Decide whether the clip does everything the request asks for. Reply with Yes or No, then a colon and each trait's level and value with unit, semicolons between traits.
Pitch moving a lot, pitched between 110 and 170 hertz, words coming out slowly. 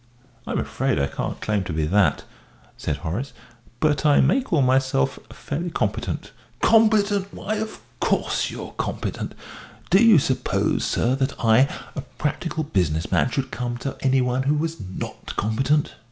No: wide, 6.6 semitones; low, 135 Hz; average, 155 wpm